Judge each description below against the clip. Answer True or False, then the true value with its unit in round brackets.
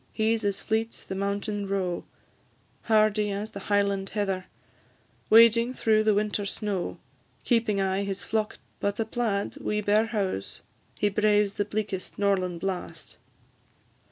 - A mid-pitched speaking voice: False (205 Hz)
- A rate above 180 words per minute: False (150 wpm)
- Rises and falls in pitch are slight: True (1.6 semitones)